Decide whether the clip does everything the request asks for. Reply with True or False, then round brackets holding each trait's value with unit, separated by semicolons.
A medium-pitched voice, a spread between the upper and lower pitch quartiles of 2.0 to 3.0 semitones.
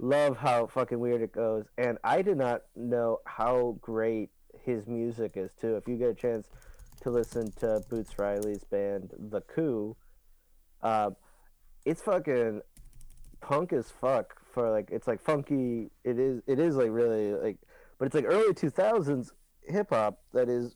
False (120 Hz; 2.6 semitones)